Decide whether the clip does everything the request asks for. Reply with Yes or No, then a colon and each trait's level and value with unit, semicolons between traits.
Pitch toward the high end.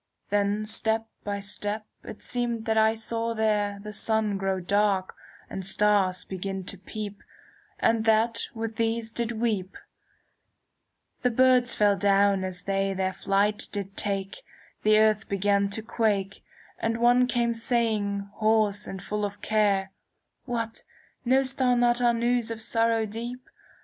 Yes: high, 215 Hz